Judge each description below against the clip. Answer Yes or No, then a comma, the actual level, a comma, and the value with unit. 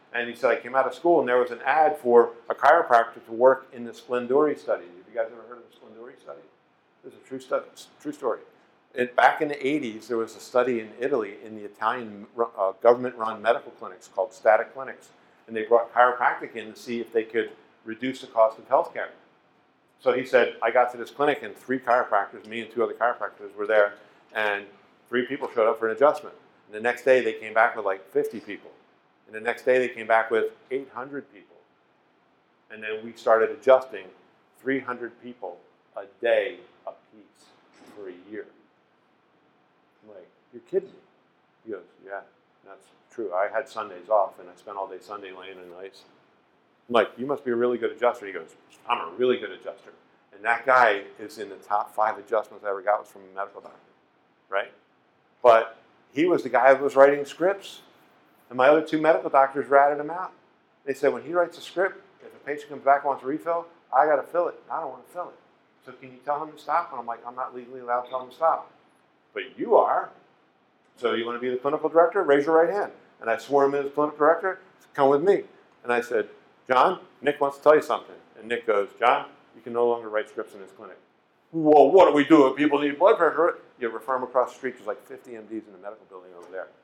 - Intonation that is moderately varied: Yes, average, 4.3 semitones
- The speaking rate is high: Yes, fast, 230 wpm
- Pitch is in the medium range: No, low, 125 Hz